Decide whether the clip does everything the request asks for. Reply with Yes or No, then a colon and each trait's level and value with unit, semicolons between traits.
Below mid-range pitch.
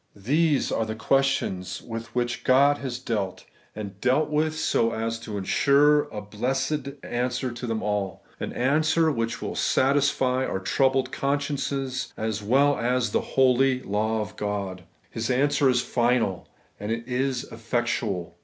Yes: low, 125 Hz